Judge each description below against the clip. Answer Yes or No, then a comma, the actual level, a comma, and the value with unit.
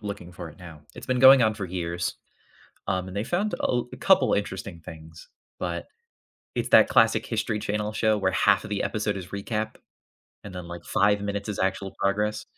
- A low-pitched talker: Yes, low, 100 Hz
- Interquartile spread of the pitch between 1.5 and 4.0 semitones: Yes, average, 2.7 semitones